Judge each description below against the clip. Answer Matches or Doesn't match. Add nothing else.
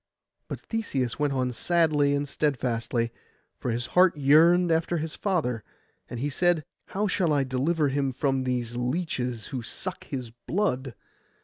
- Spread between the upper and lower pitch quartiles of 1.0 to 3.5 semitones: Doesn't match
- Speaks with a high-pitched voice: Doesn't match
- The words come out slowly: Doesn't match